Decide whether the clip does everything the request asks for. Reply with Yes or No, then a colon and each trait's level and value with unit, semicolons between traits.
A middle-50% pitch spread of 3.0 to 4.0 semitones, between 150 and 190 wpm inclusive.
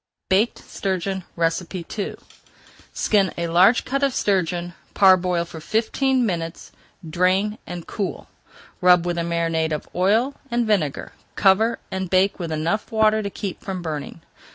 No: average, 3.7 semitones; average, 140 wpm